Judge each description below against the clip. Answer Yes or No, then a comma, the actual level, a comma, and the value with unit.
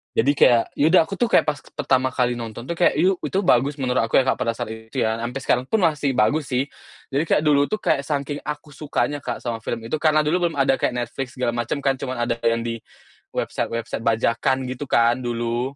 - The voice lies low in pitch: Yes, low, 130 Hz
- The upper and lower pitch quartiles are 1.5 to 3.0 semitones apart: No, average, 3.7 semitones